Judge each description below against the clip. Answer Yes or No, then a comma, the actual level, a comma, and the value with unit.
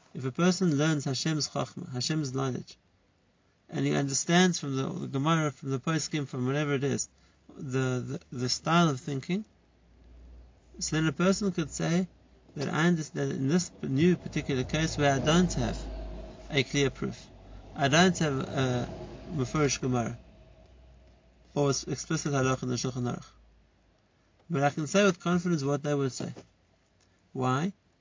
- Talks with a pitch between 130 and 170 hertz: Yes, medium, 140 Hz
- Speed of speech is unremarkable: Yes, average, 160 wpm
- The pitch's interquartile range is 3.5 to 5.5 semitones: Yes, average, 4.3 semitones